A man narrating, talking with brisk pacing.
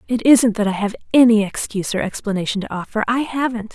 No: female; fast, 210 wpm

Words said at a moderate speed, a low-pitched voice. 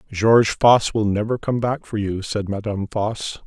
Yes: average, 190 wpm; low, 110 Hz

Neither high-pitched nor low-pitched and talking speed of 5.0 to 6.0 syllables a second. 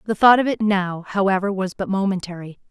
No: high, 195 Hz; 5.9 syllables/s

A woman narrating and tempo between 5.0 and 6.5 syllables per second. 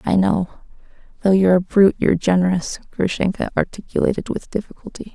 Yes: female; 6.3 syllables/s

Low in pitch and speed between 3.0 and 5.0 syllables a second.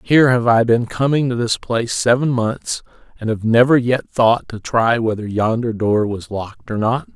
Yes: low, 115 Hz; 4.8 syllables/s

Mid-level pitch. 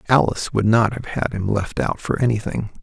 No: low, 110 Hz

